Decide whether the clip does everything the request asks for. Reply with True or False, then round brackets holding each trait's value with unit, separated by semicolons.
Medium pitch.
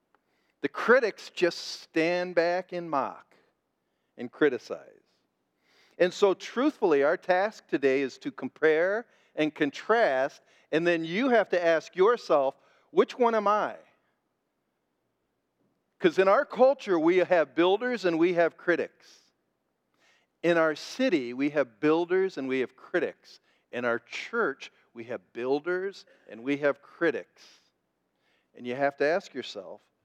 True (175 Hz)